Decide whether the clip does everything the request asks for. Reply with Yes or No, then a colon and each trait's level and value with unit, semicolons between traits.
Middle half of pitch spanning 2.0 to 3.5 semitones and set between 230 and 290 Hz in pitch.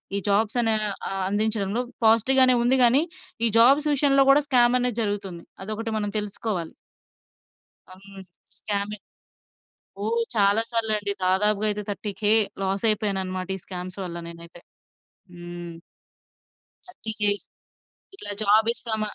No: average, 2.9 semitones; high, 210 Hz